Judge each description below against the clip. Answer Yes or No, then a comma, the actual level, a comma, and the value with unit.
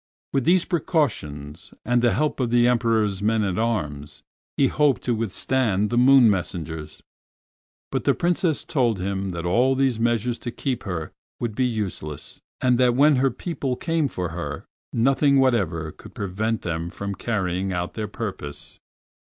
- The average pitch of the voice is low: Yes, low, 115 Hz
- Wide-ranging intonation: Yes, wide, 5.8 semitones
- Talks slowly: No, average, 160 wpm